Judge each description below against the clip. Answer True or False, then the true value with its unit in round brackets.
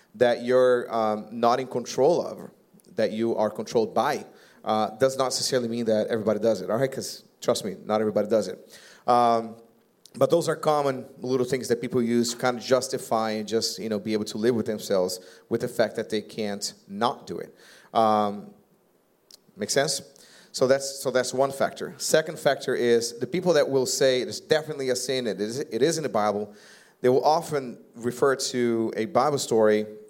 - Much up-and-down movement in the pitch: False (3.3 semitones)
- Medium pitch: False (120 Hz)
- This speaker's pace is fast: False (195 wpm)